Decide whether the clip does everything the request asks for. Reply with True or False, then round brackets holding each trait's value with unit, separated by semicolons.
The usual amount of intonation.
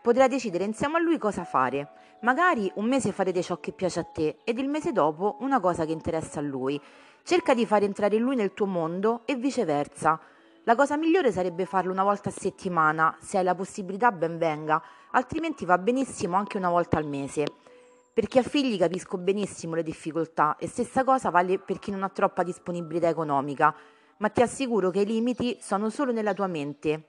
False (6.5 semitones)